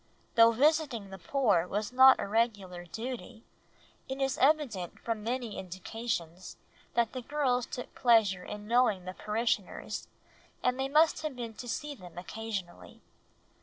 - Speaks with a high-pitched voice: Yes, high, 230 Hz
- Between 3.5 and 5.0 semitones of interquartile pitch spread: Yes, average, 4.6 semitones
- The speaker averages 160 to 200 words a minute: No, average, 145 wpm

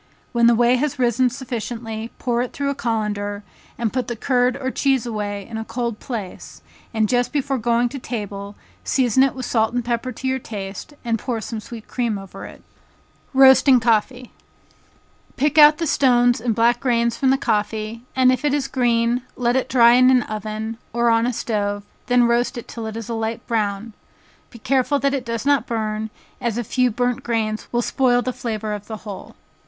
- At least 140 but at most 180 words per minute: No, average, 200 wpm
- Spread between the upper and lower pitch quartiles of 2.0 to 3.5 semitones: Yes, narrow, 2.5 semitones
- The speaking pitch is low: No, high, 235 Hz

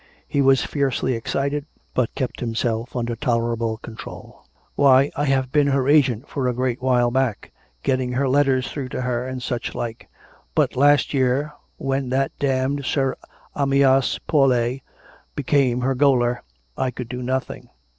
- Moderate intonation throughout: No, narrow, 2.0 semitones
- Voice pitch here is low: Yes, low, 130 Hz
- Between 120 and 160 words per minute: Yes, average, 155 wpm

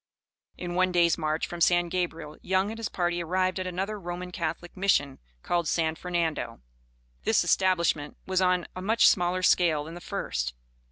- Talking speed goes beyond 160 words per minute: Yes, average, 170 wpm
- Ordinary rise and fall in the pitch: No, narrow, 2.0 semitones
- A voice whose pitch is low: No, medium, 175 Hz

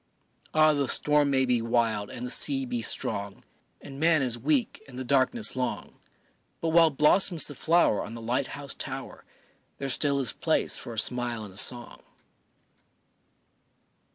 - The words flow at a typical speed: Yes, average, 165 wpm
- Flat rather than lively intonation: No, average, 3.8 semitones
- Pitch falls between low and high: No, low, 130 Hz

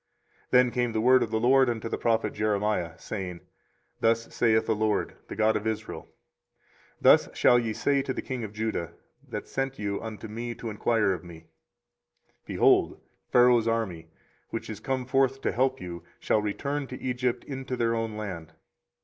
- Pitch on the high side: No, low, 115 Hz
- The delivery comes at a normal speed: Yes, average, 185 wpm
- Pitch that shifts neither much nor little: Yes, average, 3.0 semitones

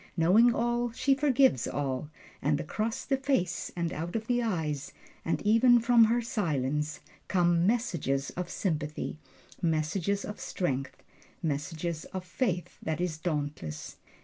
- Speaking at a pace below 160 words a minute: Yes, average, 140 wpm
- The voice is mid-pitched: Yes, medium, 175 Hz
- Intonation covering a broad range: Yes, wide, 7.0 semitones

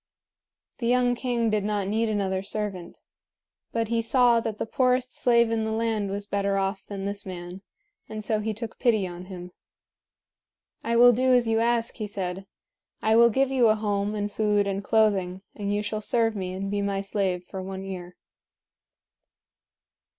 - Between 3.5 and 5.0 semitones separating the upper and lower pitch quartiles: No, average, 2.8 semitones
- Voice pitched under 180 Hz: No, high, 210 Hz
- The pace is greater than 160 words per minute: Yes, average, 180 wpm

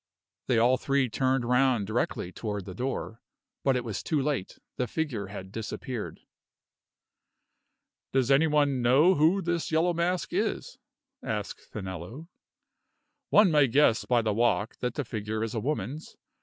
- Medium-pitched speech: No, low, 125 Hz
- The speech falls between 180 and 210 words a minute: No, average, 150 wpm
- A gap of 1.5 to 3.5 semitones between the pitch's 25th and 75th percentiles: No, average, 5.0 semitones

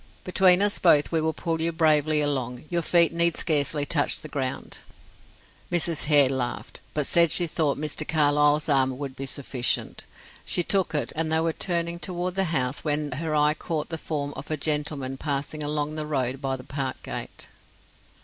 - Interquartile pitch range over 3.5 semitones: No, average, 2.7 semitones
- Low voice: No, medium, 150 Hz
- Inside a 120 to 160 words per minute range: No, average, 185 wpm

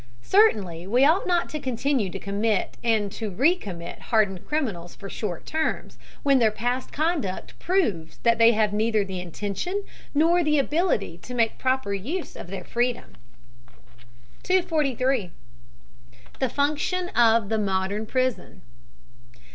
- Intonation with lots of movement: Yes, wide, 6.7 semitones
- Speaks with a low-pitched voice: No, high, 230 Hz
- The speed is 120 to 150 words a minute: Yes, average, 140 wpm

